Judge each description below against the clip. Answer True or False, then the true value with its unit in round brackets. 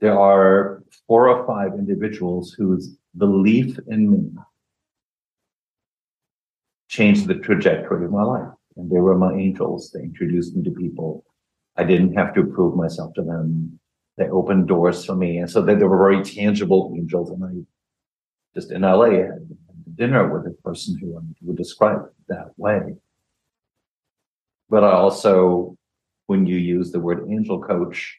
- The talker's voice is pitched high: False (95 Hz)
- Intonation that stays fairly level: False (3.1 semitones)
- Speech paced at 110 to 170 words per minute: True (155 wpm)